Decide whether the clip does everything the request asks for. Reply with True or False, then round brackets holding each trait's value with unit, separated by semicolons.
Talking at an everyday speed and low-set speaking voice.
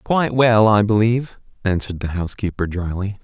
True (150 wpm; 105 Hz)